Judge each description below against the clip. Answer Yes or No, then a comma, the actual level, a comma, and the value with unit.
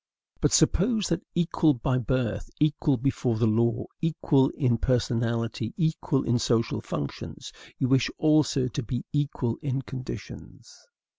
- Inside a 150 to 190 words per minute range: No, slow, 135 wpm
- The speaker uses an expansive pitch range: No, average, 4.1 semitones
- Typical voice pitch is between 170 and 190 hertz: No, low, 130 Hz